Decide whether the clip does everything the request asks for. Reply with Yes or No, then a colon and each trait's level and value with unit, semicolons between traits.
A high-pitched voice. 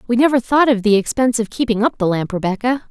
Yes: high, 230 Hz